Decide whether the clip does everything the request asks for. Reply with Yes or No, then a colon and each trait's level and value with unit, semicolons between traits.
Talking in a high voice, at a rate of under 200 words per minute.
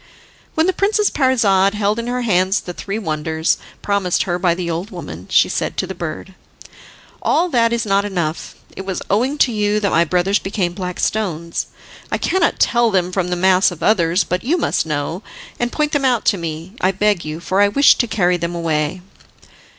No: high, 195 Hz; fast, 205 wpm